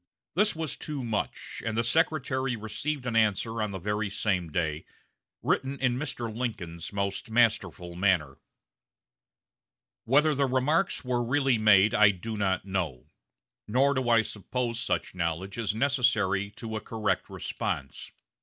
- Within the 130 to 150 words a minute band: Yes, average, 145 wpm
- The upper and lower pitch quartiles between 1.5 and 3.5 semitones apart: No, average, 4.8 semitones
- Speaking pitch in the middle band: No, low, 110 Hz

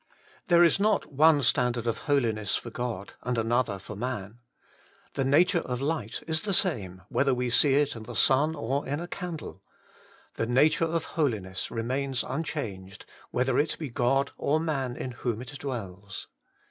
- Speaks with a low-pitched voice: Yes, low, 130 Hz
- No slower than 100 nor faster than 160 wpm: No, average, 170 wpm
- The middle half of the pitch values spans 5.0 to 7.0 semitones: No, average, 4.6 semitones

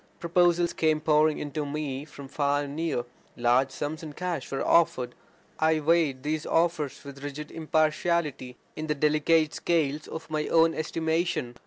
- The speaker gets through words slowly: No, average, 160 wpm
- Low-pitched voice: No, medium, 155 Hz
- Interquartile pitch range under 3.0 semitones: Yes, narrow, 2.4 semitones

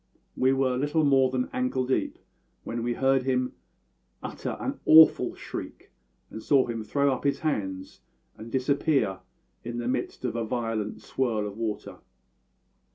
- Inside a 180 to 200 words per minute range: No, average, 155 wpm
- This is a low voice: Yes, low, 125 Hz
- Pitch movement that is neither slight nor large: Yes, average, 3.0 semitones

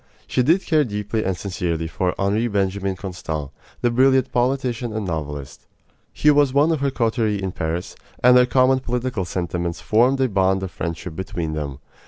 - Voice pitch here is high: No, low, 105 Hz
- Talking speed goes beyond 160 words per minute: Yes, average, 175 wpm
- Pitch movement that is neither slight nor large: No, wide, 6.4 semitones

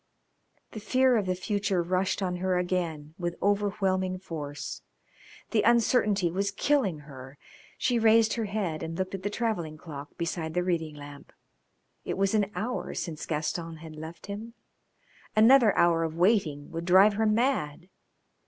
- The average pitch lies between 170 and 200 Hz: Yes, medium, 185 Hz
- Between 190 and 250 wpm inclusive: No, average, 155 wpm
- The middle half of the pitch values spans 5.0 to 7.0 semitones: No, average, 4.4 semitones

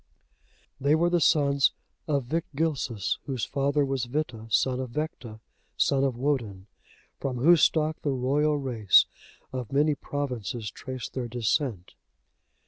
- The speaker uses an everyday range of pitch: Yes, average, 3.5 semitones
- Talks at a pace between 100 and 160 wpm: Yes, slow, 135 wpm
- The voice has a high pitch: No, low, 135 Hz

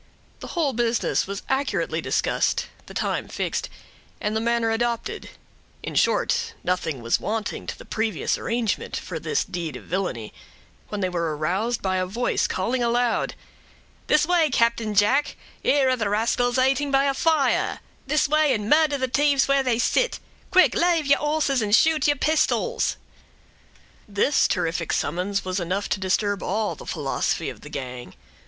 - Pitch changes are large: Yes, wide, 6.6 semitones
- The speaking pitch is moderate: No, high, 230 Hz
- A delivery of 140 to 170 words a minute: Yes, average, 160 wpm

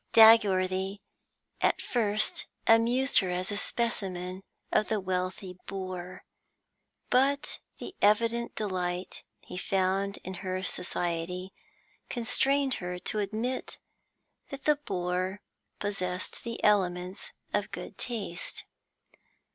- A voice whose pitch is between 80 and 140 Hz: No, high, 195 Hz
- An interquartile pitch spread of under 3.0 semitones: No, average, 3.7 semitones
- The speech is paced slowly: Yes, slow, 105 wpm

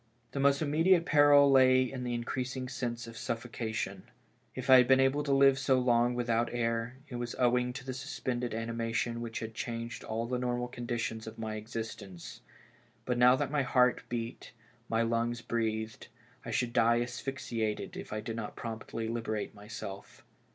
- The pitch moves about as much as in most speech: No, narrow, 2.0 semitones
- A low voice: Yes, low, 120 Hz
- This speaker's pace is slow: No, average, 175 wpm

